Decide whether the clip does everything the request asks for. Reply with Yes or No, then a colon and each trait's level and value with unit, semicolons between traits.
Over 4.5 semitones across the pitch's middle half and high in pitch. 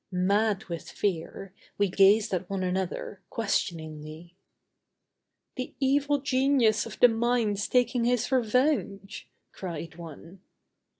Yes: wide, 5.4 semitones; high, 205 Hz